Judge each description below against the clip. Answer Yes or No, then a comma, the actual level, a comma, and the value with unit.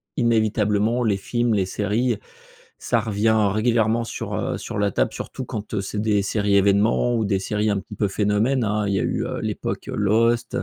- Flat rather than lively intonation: Yes, narrow, 2.1 semitones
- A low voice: Yes, low, 105 Hz